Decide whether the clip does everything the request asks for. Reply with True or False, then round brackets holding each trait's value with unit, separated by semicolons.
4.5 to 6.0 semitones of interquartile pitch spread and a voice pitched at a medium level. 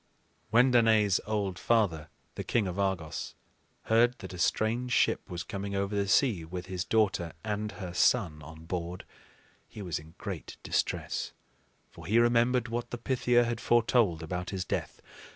False (4.9 semitones; 100 Hz)